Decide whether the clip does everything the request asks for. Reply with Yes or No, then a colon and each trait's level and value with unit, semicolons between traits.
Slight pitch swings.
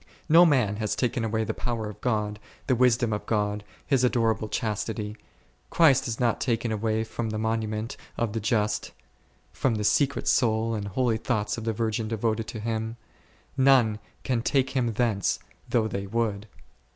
Yes: narrow, 2.1 semitones